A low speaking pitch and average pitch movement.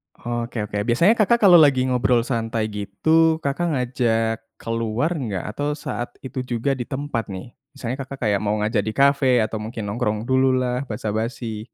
Yes: low, 120 Hz; average, 3.7 semitones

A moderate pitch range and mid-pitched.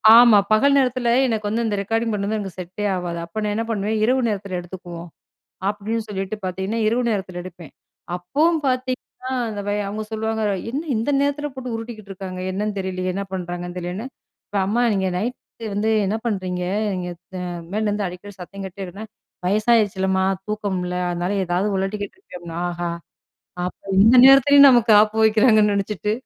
No: average, 3.3 semitones; high, 205 Hz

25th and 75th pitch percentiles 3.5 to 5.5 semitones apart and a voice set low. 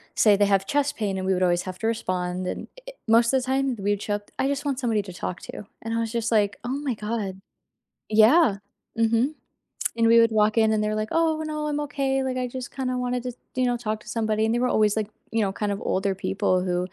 No: average, 3.8 semitones; high, 225 Hz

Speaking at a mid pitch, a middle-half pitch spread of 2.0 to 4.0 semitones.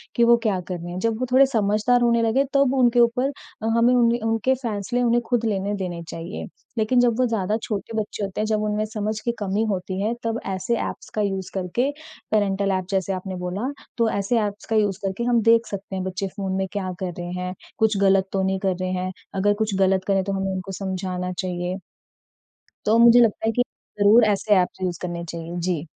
No: high, 205 Hz; average, 3.4 semitones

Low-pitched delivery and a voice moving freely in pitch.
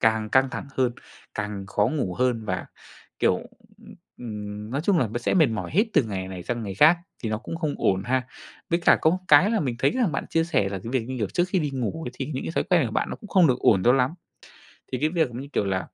Yes: low, 125 Hz; wide, 6.7 semitones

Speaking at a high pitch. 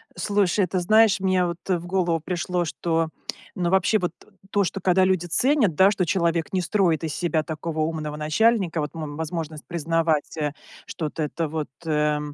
No: medium, 170 Hz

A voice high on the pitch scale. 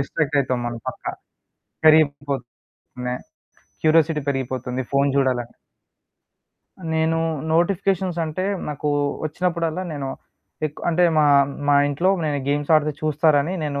No: medium, 150 Hz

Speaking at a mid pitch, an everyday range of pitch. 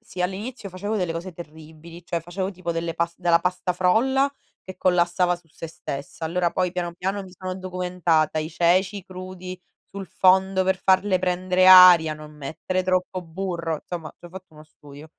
No: medium, 180 Hz; narrow, 1.8 semitones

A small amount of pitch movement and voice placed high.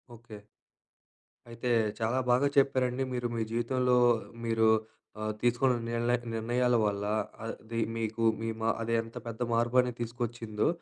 No: narrow, 1.5 semitones; low, 115 Hz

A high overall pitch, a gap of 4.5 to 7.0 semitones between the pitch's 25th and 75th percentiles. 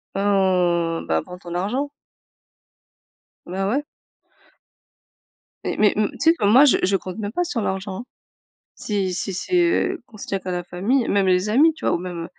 Yes: high, 195 Hz; average, 5.0 semitones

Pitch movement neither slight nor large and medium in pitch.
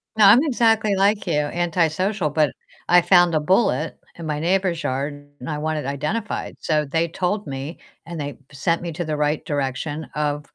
Yes: average, 4.1 semitones; medium, 160 Hz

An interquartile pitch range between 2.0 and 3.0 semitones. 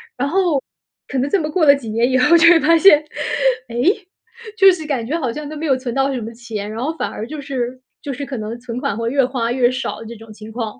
No: average, 4.4 semitones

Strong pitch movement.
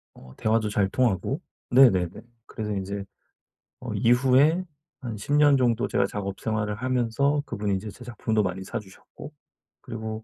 No: average, 4.0 semitones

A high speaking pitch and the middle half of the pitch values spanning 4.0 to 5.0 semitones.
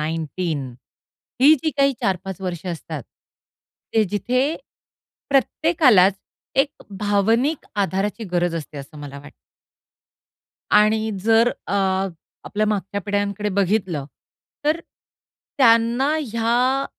Yes: high, 210 Hz; average, 4.6 semitones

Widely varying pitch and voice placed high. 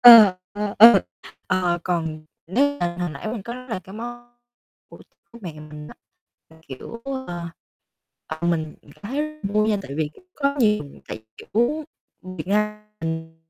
Yes: wide, 6.6 semitones; high, 205 Hz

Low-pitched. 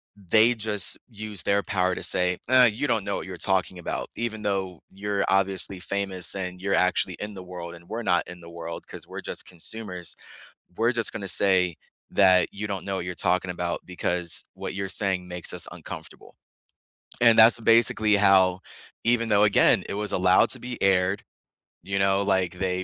Yes: very low, 95 Hz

